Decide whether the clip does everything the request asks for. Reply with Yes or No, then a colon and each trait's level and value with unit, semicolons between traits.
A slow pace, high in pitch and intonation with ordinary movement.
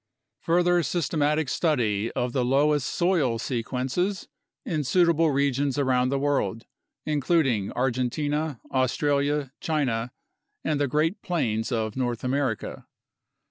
No: slow, 110 wpm; medium, 140 Hz; average, 3.7 semitones